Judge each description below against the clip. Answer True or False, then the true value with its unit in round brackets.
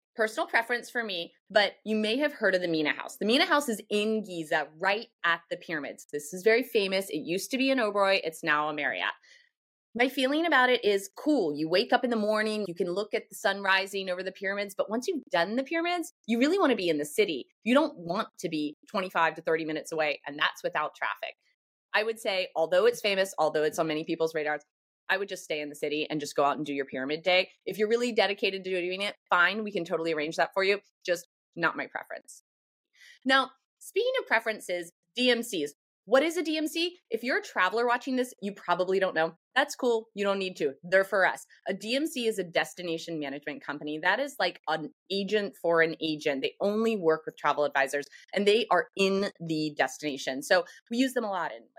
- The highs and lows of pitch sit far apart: True (6.6 semitones)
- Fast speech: True (225 wpm)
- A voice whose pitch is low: False (195 Hz)